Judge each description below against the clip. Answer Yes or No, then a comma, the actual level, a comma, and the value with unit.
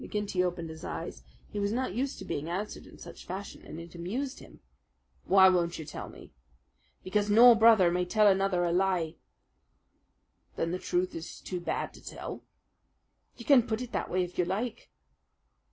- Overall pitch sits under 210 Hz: Yes, medium, 185 Hz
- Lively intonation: No, average, 3.5 semitones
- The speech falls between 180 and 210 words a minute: Yes, average, 185 wpm